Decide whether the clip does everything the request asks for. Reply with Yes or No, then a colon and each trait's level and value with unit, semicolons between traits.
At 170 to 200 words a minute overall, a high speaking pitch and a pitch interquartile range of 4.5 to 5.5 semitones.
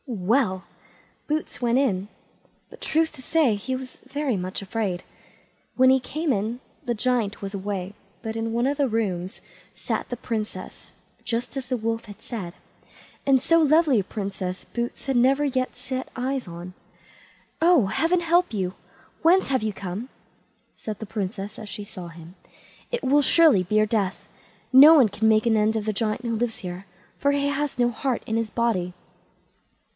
Yes: average, 180 wpm; high, 230 Hz; average, 4.8 semitones